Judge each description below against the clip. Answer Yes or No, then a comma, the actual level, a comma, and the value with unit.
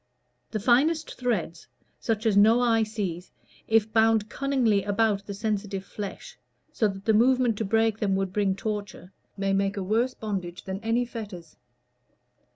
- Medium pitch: No, high, 215 Hz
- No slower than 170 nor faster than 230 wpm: No, average, 160 wpm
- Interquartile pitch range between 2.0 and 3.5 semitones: Yes, narrow, 2.5 semitones